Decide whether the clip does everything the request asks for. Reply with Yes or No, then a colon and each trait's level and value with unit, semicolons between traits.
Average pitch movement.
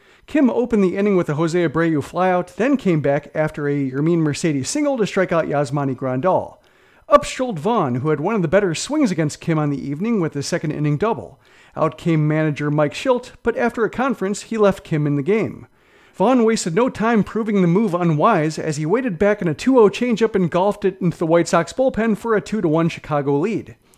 No: wide, 6.2 semitones